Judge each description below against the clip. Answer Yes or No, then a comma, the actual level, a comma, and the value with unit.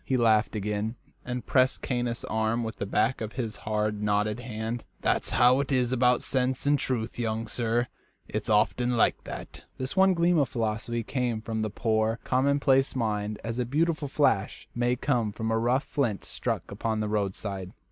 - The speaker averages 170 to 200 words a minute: Yes, average, 180 wpm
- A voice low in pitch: Yes, low, 115 Hz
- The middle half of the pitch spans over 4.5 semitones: No, average, 2.9 semitones